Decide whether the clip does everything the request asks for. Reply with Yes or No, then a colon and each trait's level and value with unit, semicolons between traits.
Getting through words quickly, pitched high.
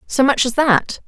Yes: fast, 225 wpm; very high, 260 Hz